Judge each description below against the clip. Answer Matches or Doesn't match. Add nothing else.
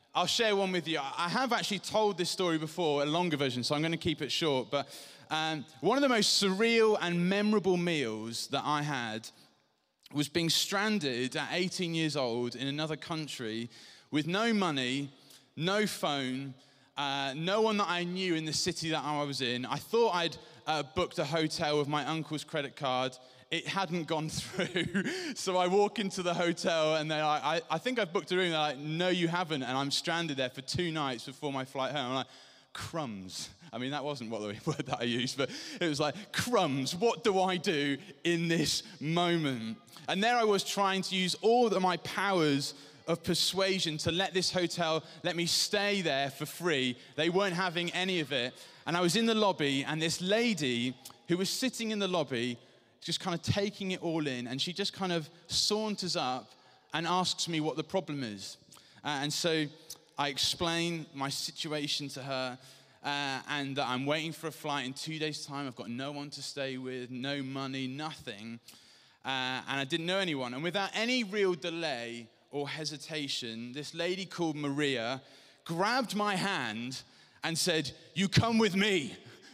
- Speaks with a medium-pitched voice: Matches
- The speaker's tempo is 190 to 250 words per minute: Matches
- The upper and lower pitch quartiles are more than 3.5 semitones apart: Matches